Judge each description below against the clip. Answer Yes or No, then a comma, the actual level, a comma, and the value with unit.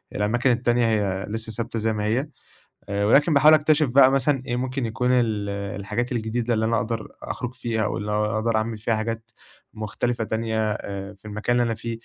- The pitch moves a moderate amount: No, narrow, 2.3 semitones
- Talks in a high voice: No, low, 115 Hz